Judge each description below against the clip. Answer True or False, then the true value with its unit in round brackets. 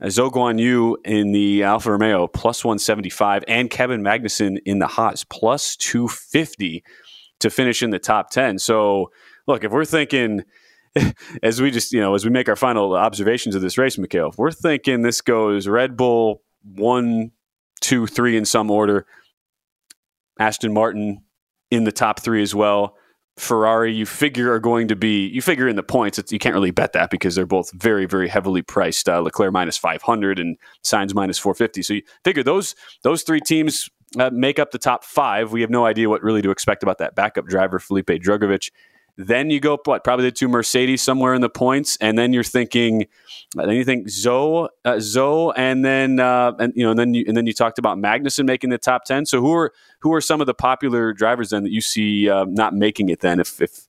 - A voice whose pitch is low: True (115 Hz)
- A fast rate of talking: True (210 wpm)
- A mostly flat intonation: False (3.5 semitones)